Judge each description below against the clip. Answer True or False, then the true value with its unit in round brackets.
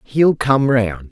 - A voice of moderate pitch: False (125 Hz)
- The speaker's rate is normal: True (160 wpm)